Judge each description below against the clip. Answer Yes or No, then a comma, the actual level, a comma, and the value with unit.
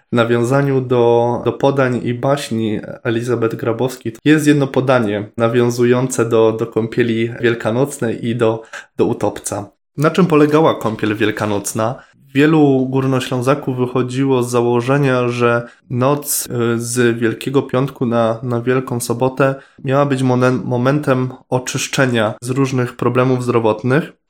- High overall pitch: No, low, 125 Hz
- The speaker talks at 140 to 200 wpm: No, average, 120 wpm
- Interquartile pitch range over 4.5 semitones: No, narrow, 2.5 semitones